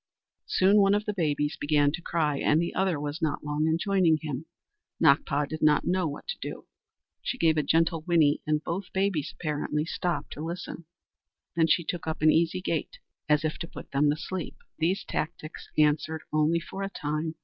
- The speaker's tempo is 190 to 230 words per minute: Yes, average, 195 wpm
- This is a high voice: No, medium, 160 Hz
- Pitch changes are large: No, narrow, 2.5 semitones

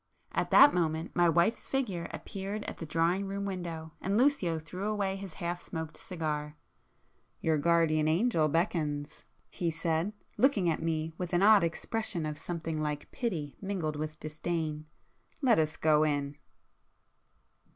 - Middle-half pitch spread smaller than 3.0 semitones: No, average, 3.7 semitones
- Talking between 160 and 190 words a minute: No, average, 140 wpm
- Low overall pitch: No, medium, 165 Hz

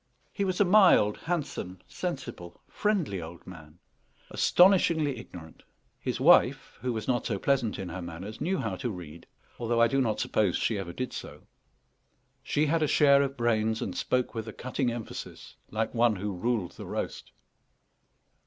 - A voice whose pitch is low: Yes, low, 115 Hz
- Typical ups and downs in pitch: No, wide, 6.3 semitones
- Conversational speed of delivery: Yes, average, 170 wpm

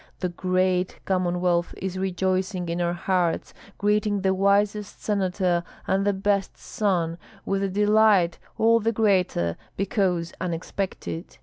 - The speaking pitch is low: No, high, 190 Hz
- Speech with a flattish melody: Yes, narrow, 2.2 semitones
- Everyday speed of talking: No, slow, 125 wpm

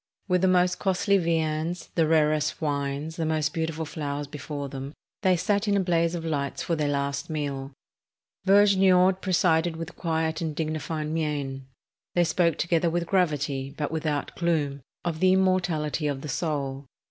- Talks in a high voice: No, medium, 160 Hz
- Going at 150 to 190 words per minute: Yes, average, 160 wpm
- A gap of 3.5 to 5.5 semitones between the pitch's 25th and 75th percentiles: No, average, 3.1 semitones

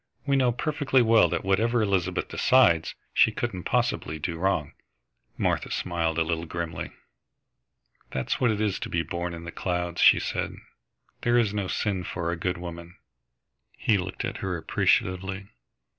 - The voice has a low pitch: Yes, very low, 90 Hz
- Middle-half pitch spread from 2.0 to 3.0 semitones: No, average, 3.9 semitones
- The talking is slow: No, average, 160 wpm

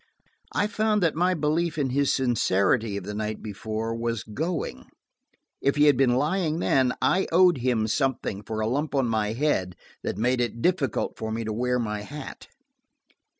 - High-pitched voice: No, low, 125 Hz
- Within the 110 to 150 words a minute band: No, average, 180 wpm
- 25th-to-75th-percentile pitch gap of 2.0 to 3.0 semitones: No, wide, 5.6 semitones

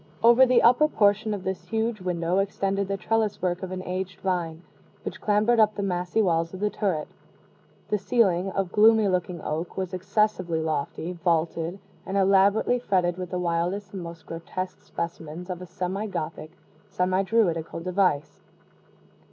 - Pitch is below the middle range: No, medium, 185 Hz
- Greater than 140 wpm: Yes, average, 160 wpm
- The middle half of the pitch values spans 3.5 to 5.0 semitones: No, average, 3.0 semitones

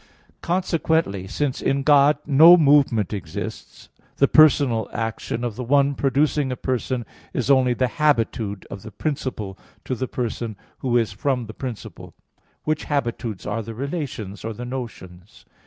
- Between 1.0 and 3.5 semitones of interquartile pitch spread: No, average, 4.2 semitones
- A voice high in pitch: No, low, 125 Hz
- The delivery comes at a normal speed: Yes, average, 150 wpm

